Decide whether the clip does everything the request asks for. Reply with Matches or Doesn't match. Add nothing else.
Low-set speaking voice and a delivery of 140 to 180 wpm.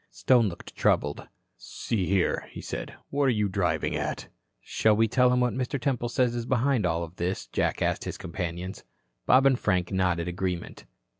Matches